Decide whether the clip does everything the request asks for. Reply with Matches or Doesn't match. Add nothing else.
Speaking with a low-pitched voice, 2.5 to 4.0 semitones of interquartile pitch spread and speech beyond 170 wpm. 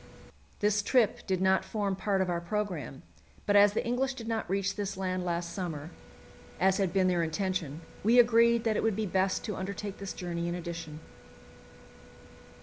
Doesn't match